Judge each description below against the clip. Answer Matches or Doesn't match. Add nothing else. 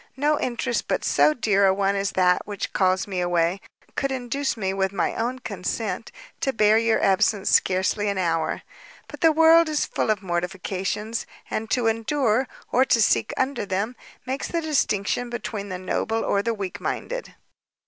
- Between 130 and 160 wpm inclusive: Doesn't match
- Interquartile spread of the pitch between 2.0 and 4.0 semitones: Doesn't match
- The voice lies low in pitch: Doesn't match